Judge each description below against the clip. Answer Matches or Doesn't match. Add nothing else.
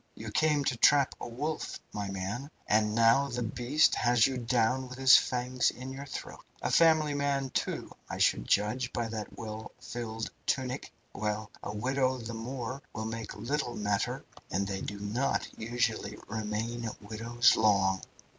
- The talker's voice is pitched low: Matches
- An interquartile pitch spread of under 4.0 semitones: Matches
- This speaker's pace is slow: Doesn't match